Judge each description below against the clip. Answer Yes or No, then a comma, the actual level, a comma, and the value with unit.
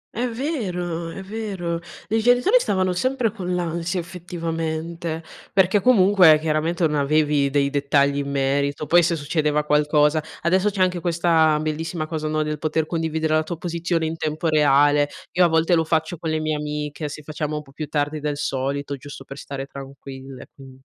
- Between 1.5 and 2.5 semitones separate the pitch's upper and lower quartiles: No, average, 2.9 semitones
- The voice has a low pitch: No, medium, 160 Hz